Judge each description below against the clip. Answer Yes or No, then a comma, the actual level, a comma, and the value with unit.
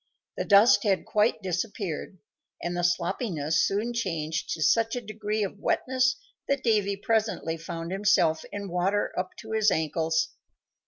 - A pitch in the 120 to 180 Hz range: No, high, 200 Hz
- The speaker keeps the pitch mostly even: No, average, 4.4 semitones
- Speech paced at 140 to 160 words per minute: Yes, average, 150 wpm